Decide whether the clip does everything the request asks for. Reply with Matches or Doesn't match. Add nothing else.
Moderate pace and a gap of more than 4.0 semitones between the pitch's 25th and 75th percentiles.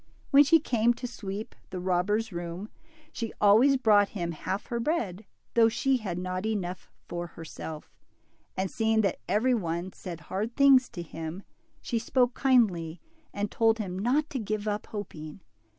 Matches